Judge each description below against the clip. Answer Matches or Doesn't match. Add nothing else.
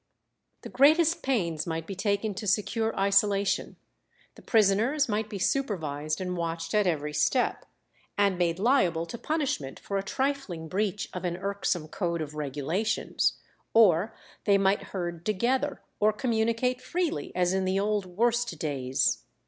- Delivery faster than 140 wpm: Matches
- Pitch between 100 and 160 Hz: Doesn't match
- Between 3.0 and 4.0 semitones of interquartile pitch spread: Doesn't match